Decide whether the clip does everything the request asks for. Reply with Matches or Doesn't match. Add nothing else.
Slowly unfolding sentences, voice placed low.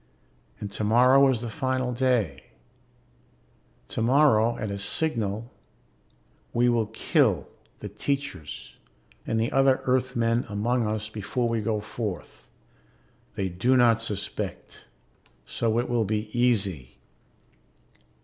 Matches